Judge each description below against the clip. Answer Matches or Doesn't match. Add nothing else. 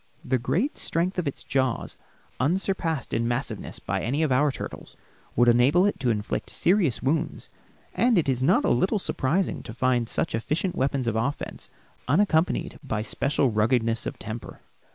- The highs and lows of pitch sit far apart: Matches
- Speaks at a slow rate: Doesn't match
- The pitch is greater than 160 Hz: Doesn't match